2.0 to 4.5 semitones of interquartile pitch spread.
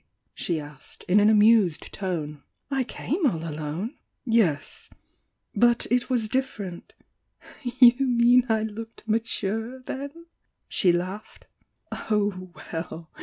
No: wide, 5.4 semitones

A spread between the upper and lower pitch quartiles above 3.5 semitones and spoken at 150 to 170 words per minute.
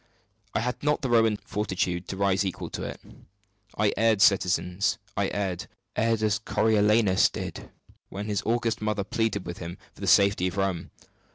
No: narrow, 2.6 semitones; average, 160 wpm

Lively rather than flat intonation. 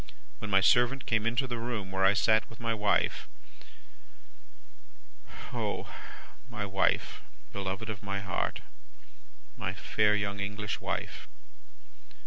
No: narrow, 2.4 semitones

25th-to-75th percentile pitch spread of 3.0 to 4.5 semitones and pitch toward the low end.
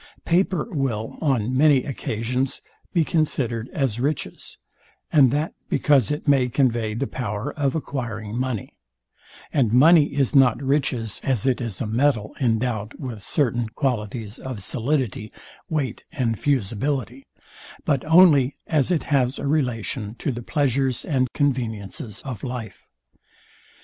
Yes: average, 3.9 semitones; low, 130 Hz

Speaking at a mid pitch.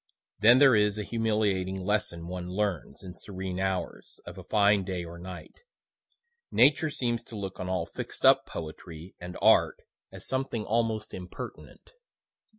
No: very low, 95 Hz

